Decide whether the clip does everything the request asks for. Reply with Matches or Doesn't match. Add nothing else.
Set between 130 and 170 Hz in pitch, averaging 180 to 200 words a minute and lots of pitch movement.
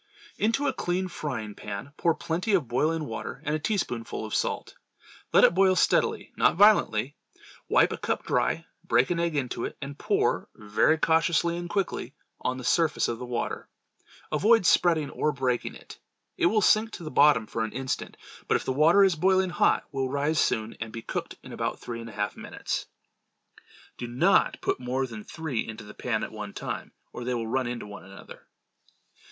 Matches